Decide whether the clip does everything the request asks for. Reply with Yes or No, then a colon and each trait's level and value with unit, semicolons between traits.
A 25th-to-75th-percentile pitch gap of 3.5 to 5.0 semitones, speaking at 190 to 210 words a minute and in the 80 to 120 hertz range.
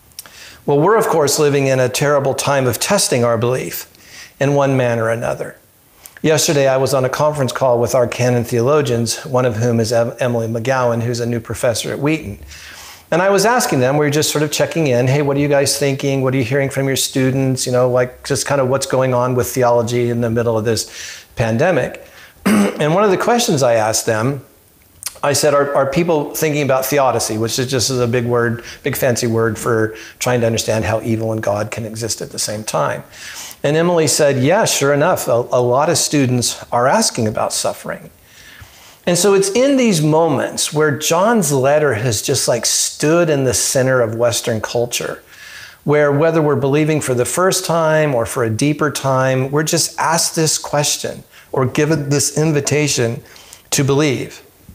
No: average, 3.9 semitones; average, 200 wpm; low, 135 Hz